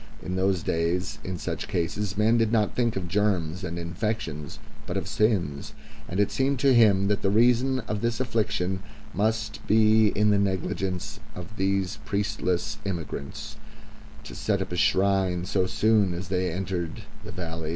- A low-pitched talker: Yes, low, 100 Hz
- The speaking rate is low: No, average, 165 wpm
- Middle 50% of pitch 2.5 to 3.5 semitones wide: Yes, average, 3.2 semitones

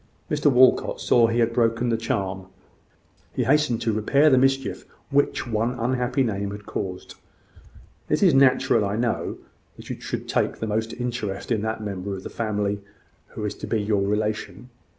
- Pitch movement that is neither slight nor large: Yes, average, 3.2 semitones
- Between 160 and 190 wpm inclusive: Yes, average, 180 wpm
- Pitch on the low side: Yes, low, 115 Hz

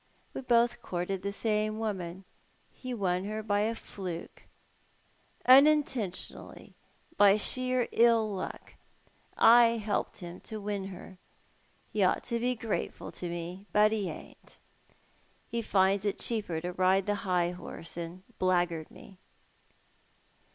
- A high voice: Yes, high, 205 Hz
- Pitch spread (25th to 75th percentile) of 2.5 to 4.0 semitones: Yes, average, 3.6 semitones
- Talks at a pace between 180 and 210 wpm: No, average, 140 wpm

